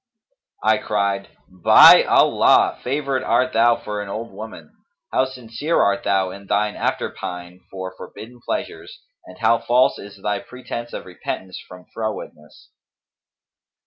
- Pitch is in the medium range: No, low, 105 Hz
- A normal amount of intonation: Yes, average, 3.6 semitones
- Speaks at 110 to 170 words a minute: Yes, average, 140 wpm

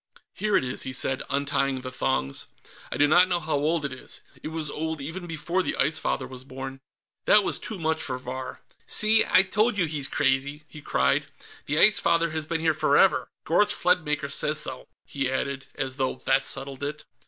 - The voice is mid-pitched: Yes, medium, 150 Hz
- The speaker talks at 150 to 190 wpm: No, average, 200 wpm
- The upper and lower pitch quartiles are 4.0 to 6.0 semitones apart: No, average, 3.6 semitones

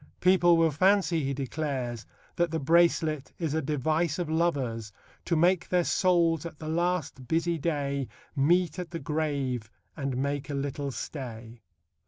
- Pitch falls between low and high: Yes, medium, 155 Hz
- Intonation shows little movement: No, average, 3.7 semitones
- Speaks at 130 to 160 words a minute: Yes, average, 155 wpm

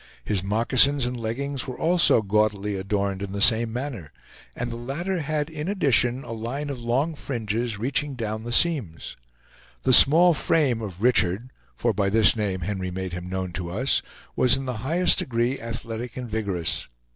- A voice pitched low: Yes, low, 115 Hz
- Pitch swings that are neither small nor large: Yes, average, 4.8 semitones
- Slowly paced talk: No, average, 175 wpm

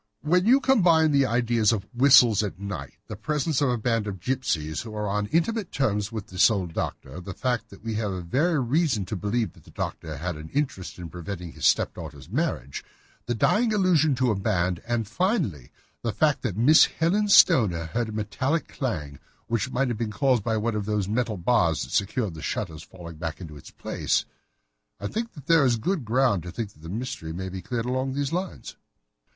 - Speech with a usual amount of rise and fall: No, wide, 6.5 semitones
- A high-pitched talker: No, low, 115 Hz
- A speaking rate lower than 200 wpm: No, fast, 205 wpm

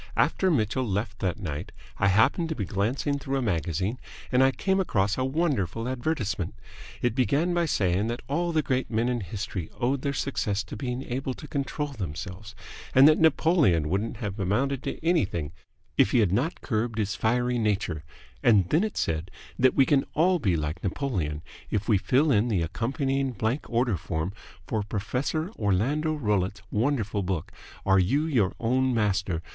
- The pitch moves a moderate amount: No, wide, 5.9 semitones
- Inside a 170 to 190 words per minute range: Yes, average, 175 wpm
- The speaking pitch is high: No, low, 115 Hz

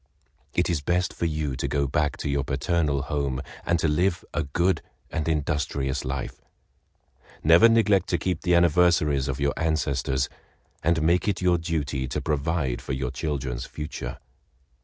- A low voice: Yes, very low, 75 Hz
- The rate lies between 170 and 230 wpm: No, average, 160 wpm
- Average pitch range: Yes, average, 3.6 semitones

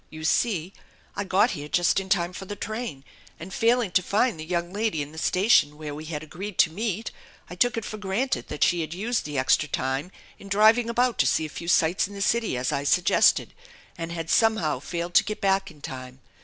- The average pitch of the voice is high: No, medium, 180 Hz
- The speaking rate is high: Yes, fast, 225 wpm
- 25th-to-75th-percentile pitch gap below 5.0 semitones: No, average, 5.3 semitones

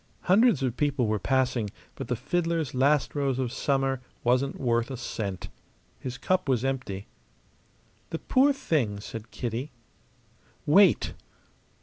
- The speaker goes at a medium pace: No, slow, 130 wpm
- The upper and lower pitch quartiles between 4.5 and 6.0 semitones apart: No, average, 4.1 semitones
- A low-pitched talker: Yes, low, 130 Hz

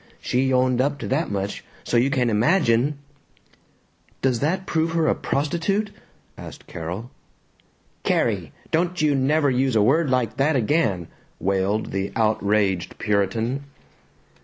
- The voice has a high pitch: No, low, 130 Hz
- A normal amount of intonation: No, wide, 5.8 semitones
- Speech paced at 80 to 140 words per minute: Yes, slow, 135 wpm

